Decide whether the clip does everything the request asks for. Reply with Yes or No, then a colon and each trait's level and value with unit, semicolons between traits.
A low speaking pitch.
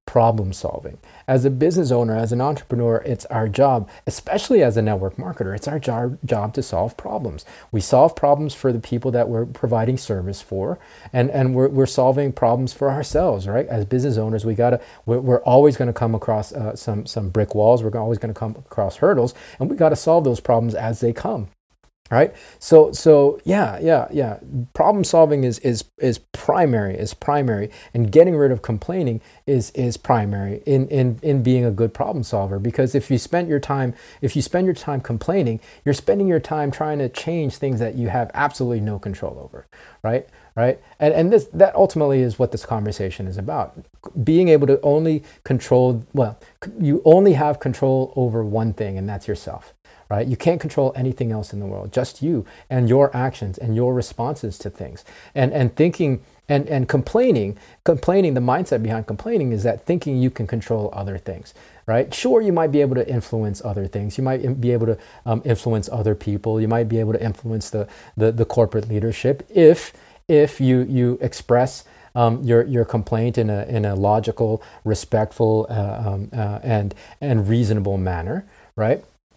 Yes: low, 120 Hz